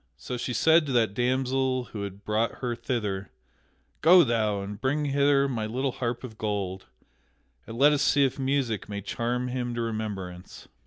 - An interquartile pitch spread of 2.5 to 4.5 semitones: Yes, average, 3.9 semitones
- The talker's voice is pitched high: No, low, 120 Hz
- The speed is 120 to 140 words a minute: No, average, 175 wpm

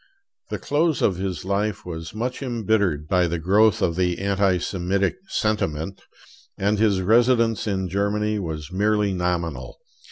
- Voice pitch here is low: Yes, low, 100 Hz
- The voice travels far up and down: No, average, 3.3 semitones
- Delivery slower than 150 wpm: Yes, average, 140 wpm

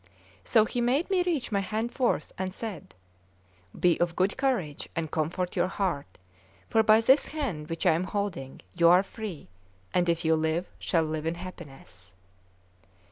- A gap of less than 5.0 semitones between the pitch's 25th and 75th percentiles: No, wide, 5.5 semitones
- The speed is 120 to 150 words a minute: No, average, 170 wpm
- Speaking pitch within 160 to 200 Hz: Yes, medium, 185 Hz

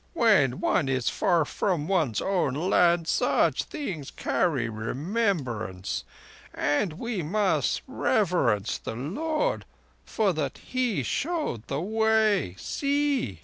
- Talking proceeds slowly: Yes, slow, 110 wpm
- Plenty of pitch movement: Yes, wide, 8.6 semitones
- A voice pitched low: No, medium, 175 Hz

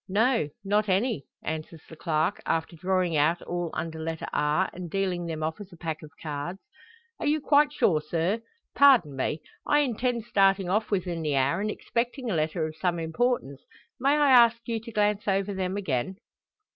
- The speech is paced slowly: No, average, 185 wpm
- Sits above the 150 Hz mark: Yes, medium, 185 Hz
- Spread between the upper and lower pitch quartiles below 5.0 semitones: No, wide, 5.5 semitones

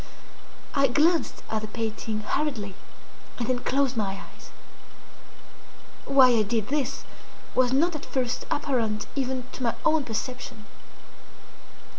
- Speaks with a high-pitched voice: Yes, very high, 250 Hz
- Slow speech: Yes, slow, 125 wpm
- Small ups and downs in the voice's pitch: No, average, 3.9 semitones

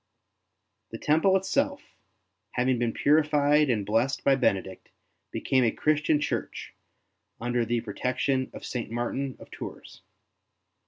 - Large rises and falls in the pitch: No, average, 4.0 semitones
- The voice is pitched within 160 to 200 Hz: No, low, 130 Hz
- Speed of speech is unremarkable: No, slow, 125 wpm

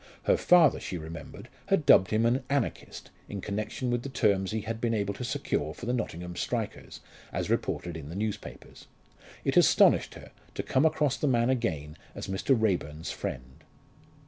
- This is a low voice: Yes, low, 110 Hz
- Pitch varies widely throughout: Yes, wide, 5.8 semitones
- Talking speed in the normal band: Yes, average, 175 wpm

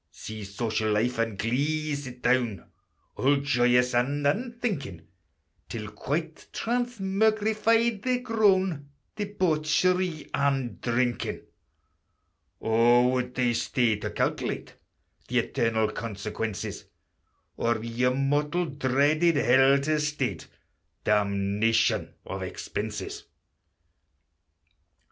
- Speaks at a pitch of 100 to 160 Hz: Yes, low, 135 Hz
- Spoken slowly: Yes, slow, 90 wpm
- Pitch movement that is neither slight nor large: No, wide, 6.2 semitones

